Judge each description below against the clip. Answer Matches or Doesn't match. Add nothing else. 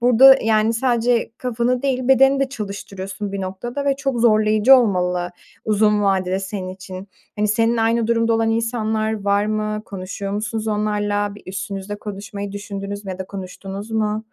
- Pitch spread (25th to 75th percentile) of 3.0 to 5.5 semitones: Doesn't match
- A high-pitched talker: Matches